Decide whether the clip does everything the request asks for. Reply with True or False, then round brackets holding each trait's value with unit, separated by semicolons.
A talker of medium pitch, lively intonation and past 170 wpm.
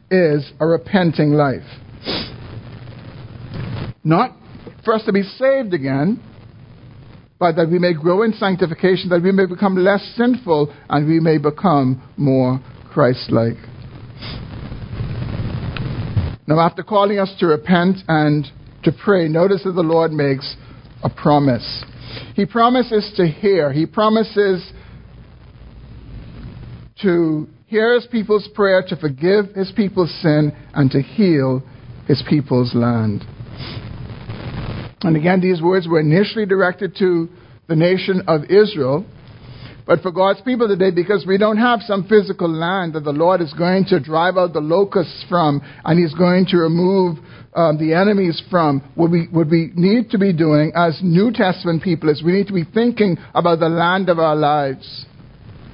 False (165 Hz; 5.9 semitones; 145 wpm)